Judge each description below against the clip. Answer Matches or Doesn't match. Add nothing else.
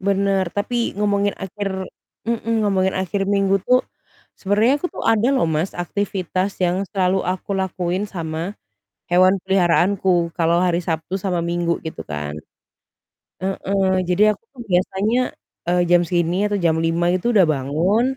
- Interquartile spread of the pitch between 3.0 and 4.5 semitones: Doesn't match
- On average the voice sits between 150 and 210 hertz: Matches